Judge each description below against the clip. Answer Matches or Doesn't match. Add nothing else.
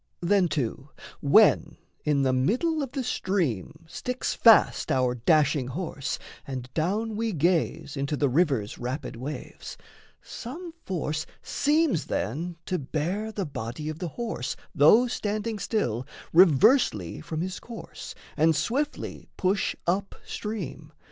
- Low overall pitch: Doesn't match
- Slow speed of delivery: Matches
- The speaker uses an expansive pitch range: Matches